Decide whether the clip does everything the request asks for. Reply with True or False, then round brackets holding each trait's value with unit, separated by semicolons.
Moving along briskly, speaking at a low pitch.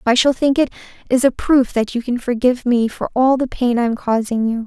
False (255 wpm; 245 Hz)